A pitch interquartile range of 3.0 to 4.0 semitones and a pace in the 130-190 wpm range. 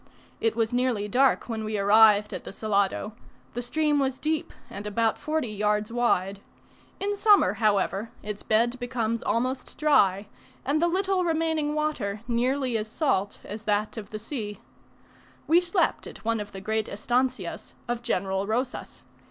No: average, 4.6 semitones; average, 160 wpm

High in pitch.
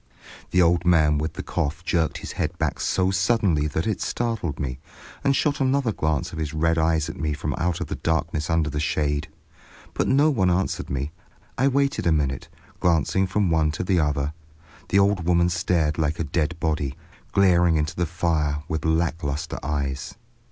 No: very low, 80 Hz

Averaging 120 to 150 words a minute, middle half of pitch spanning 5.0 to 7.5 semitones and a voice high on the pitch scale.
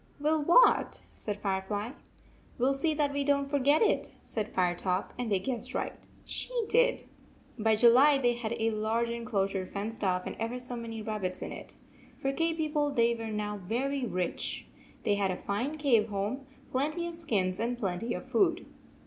No: average, 180 wpm; average, 5.3 semitones; high, 235 Hz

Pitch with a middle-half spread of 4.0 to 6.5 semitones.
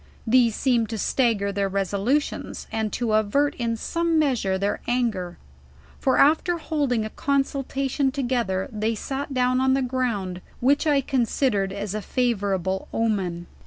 Yes: average, 4.9 semitones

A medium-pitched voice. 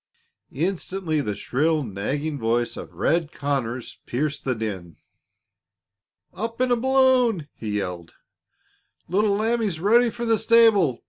Yes: medium, 160 Hz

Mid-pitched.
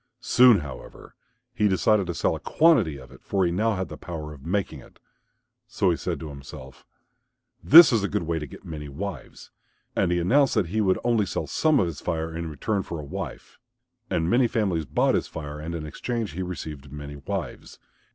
No: very low, 85 Hz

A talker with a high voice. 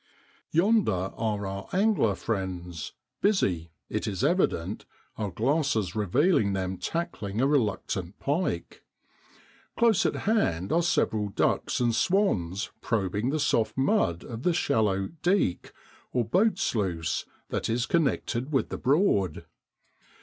No: low, 115 Hz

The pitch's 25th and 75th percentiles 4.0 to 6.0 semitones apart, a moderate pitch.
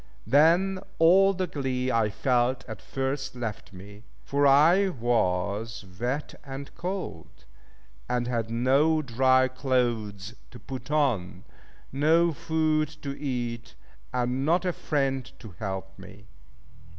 No: average, 4.7 semitones; low, 130 Hz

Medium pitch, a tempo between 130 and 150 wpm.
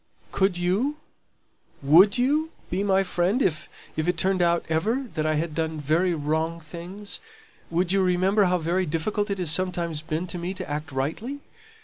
No: medium, 175 Hz; average, 175 wpm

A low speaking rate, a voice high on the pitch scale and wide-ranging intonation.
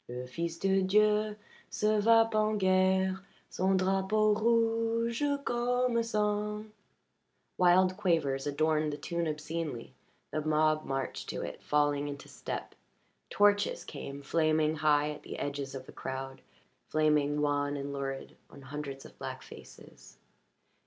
No: slow, 130 wpm; medium, 165 Hz; wide, 6.3 semitones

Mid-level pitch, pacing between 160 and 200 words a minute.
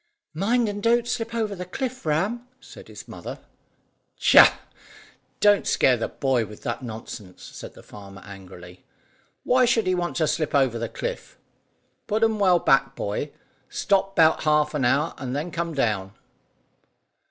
Yes: medium, 160 Hz; average, 165 wpm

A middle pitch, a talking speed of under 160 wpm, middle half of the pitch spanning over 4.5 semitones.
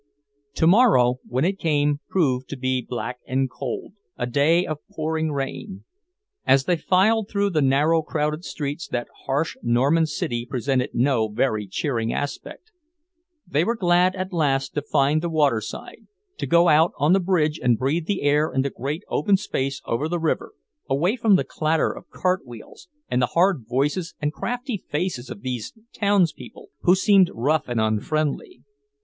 No: medium, 150 Hz; average, 165 wpm; average, 5.2 semitones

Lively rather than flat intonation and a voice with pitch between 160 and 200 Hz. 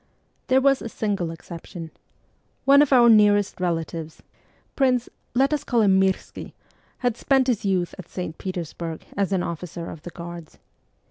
Yes: wide, 6.2 semitones; high, 190 Hz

